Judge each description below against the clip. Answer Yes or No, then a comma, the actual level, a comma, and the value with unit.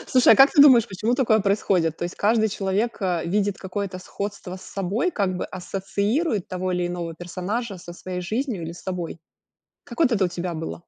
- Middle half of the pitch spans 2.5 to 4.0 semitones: Yes, average, 3.5 semitones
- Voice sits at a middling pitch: No, high, 195 Hz